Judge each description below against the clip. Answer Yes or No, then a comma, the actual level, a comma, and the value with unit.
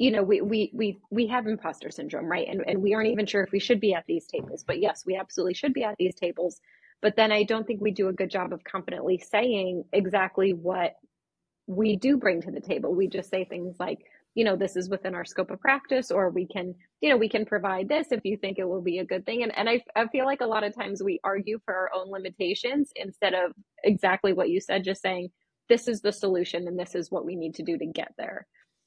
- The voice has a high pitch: Yes, high, 195 Hz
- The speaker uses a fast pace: Yes, fast, 260 wpm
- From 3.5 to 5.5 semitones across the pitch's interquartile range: No, average, 3.1 semitones